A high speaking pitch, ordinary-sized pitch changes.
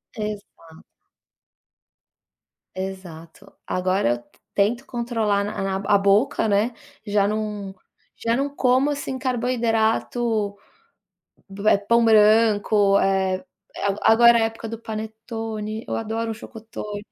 No: high, 215 Hz; narrow, 2.3 semitones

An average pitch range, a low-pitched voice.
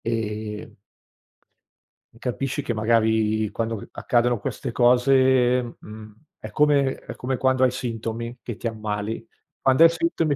Yes: average, 3.0 semitones; low, 120 Hz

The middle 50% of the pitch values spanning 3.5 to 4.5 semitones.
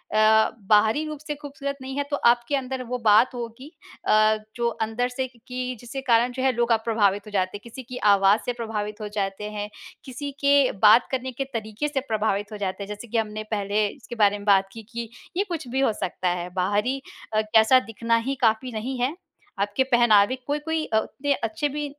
Yes: average, 3.8 semitones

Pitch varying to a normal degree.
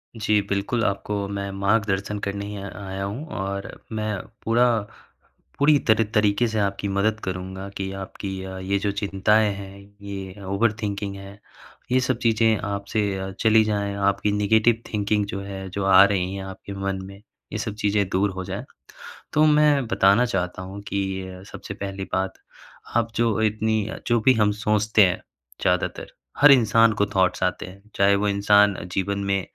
No: narrow, 1.8 semitones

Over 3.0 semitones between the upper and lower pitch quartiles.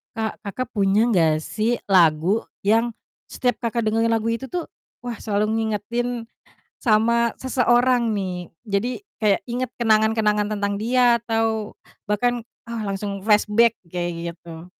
No: average, 2.7 semitones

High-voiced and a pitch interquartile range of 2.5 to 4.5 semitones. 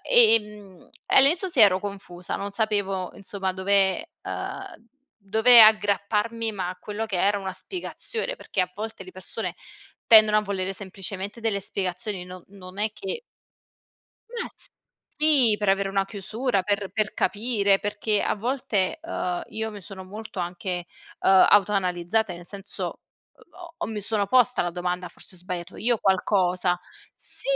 Yes: high, 200 Hz; average, 2.9 semitones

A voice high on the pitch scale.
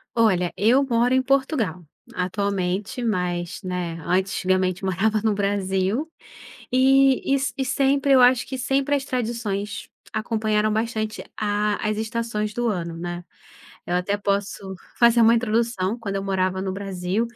Yes: high, 210 Hz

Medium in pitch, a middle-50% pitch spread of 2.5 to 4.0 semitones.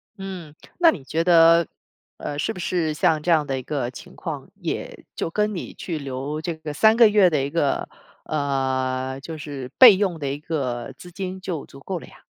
No: medium, 160 Hz; average, 4.6 semitones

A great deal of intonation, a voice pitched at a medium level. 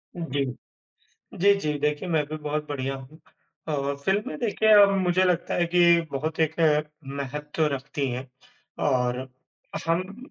No: average, 3.8 semitones; medium, 155 Hz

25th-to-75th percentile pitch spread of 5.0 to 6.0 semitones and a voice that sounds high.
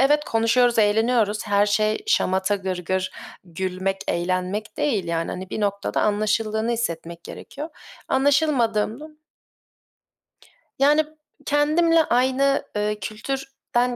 Yes: wide, 5.6 semitones; high, 215 Hz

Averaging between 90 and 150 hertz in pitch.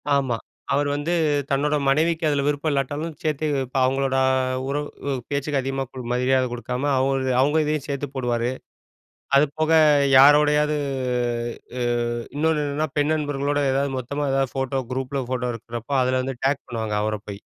Yes: medium, 140 Hz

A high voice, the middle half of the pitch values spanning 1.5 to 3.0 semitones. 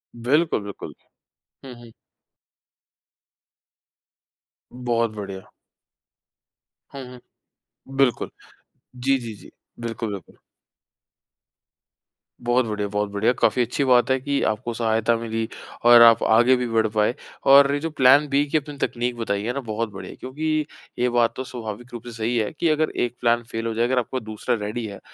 No: low, 120 Hz; average, 2.7 semitones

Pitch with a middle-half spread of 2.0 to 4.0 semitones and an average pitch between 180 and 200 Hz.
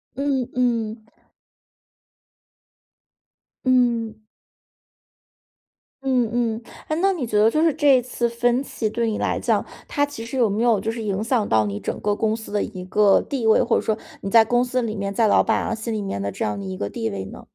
No: average, 3.0 semitones; high, 225 Hz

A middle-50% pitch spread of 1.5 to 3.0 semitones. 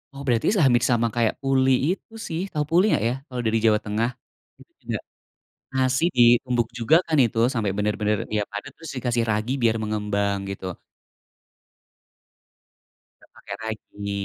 No: average, 3.6 semitones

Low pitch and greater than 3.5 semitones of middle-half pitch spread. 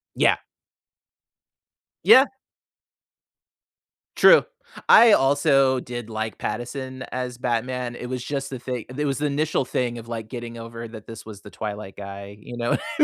No: low, 120 Hz; average, 2.8 semitones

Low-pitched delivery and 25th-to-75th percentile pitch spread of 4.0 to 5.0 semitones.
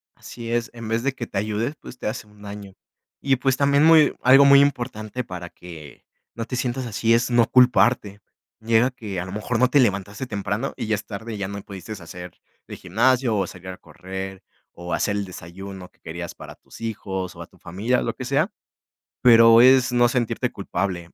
Yes: low, 110 Hz; average, 4.4 semitones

